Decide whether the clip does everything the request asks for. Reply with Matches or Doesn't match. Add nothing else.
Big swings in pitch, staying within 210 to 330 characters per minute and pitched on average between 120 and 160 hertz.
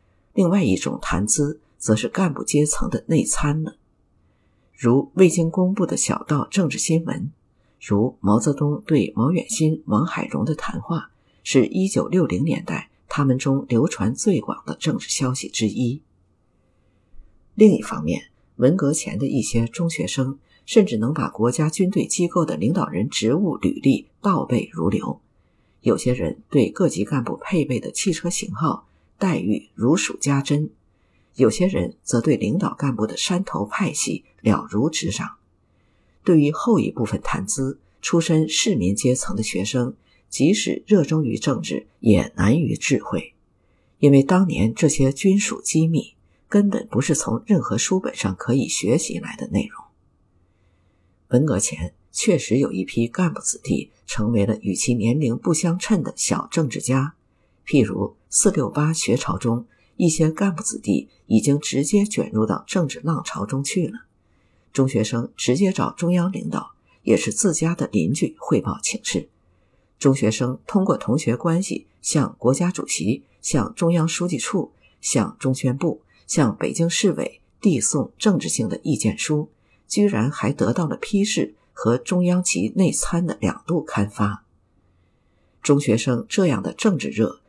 Matches